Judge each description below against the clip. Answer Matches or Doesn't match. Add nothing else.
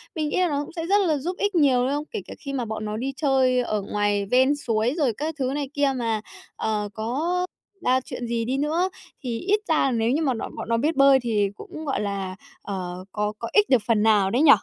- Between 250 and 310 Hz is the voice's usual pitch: Matches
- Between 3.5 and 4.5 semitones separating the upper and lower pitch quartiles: Doesn't match